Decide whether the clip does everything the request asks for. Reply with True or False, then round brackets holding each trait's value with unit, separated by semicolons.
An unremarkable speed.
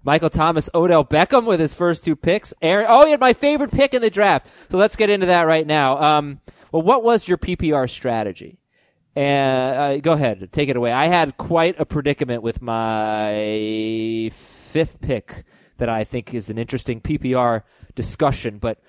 True (185 wpm)